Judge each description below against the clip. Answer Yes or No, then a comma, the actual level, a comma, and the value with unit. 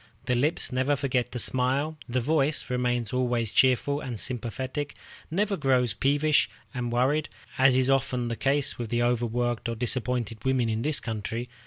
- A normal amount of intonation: No, narrow, 2.3 semitones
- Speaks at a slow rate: No, average, 165 wpm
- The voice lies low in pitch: Yes, low, 125 Hz